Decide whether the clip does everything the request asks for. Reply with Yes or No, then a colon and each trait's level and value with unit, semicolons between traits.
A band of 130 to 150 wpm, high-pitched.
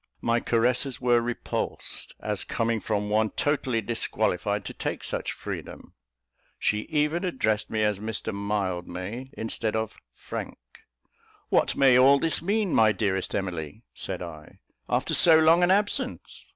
No: average, 140 wpm; low, 110 Hz